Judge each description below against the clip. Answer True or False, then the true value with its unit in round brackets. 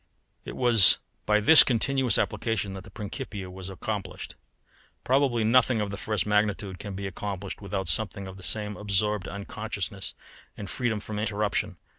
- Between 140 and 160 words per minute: True (155 wpm)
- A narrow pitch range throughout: True (2.1 semitones)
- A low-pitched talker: True (105 Hz)